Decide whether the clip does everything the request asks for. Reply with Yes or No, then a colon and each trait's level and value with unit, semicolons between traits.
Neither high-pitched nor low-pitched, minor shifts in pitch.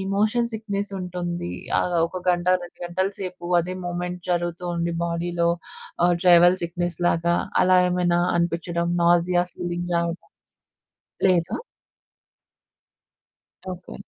Yes: medium, 175 Hz; narrow, 0.9 semitones